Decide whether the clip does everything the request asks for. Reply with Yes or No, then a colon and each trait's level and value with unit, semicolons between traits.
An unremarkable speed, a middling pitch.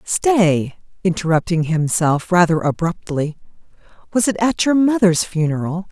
No: slow, 110 wpm; medium, 180 Hz